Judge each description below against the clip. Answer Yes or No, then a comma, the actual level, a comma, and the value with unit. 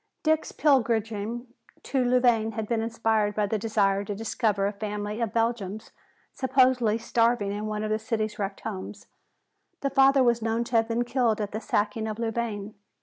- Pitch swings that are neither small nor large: No, narrow, 2.2 semitones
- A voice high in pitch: Yes, high, 225 Hz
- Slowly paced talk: No, average, 175 wpm